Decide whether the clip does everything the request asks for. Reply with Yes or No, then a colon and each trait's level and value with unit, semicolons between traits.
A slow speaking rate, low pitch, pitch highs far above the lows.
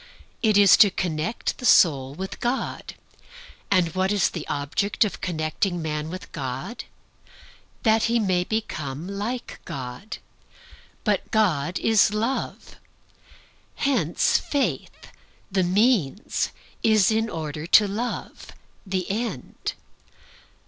No: slow, 115 wpm; high, 190 Hz; wide, 5.7 semitones